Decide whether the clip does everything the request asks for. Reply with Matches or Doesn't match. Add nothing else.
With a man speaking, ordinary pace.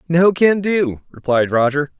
Matches